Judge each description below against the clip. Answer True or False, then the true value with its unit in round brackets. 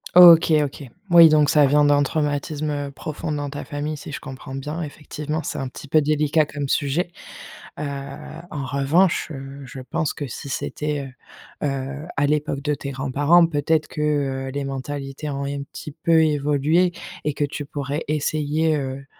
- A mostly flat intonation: True (1.8 semitones)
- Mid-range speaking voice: True (145 Hz)